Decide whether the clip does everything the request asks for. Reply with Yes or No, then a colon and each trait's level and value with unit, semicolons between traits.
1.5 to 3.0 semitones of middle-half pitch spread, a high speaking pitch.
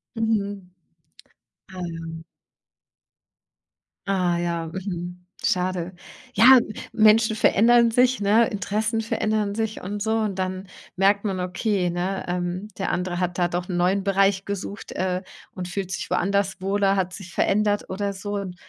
Yes: narrow, 2.4 semitones; high, 195 Hz